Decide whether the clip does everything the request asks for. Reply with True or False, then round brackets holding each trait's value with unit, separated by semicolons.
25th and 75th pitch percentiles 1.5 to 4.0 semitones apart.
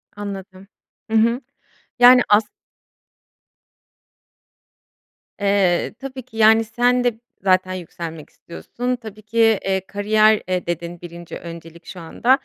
False (4.4 semitones)